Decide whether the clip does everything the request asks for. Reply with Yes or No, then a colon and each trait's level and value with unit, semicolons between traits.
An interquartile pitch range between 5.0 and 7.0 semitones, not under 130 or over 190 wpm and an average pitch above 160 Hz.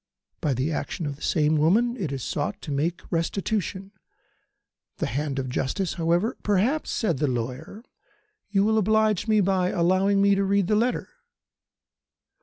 Yes: wide, 5.4 semitones; average, 165 wpm; medium, 185 Hz